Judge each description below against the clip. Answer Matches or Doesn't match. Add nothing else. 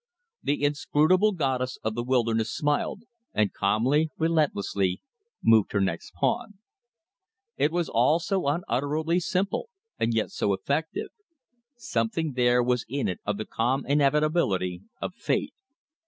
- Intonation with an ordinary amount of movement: Doesn't match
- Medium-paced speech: Doesn't match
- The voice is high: Doesn't match